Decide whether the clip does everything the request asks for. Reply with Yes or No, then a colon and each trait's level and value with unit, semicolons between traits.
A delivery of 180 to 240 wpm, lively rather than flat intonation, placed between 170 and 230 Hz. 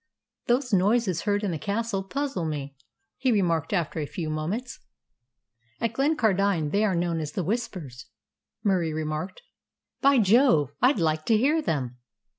No: average, 150 wpm; wide, 6.6 semitones; high, 190 Hz